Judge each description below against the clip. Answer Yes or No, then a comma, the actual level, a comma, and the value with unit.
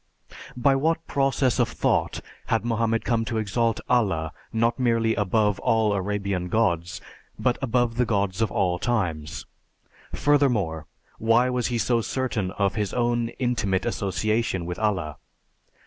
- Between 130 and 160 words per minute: Yes, average, 140 wpm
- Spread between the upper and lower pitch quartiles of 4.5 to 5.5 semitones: No, average, 3.8 semitones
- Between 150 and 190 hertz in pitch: No, low, 110 Hz